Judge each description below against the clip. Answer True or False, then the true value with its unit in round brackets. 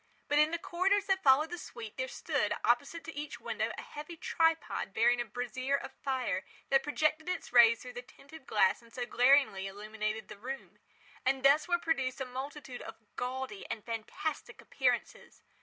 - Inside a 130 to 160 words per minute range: False (180 wpm)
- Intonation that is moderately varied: True (4.3 semitones)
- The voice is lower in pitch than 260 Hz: False (265 Hz)